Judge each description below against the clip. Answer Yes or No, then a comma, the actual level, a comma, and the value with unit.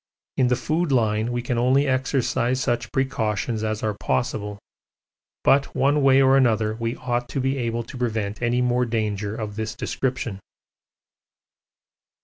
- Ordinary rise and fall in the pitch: Yes, average, 3.0 semitones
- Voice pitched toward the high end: No, low, 120 Hz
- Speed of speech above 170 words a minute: No, average, 150 wpm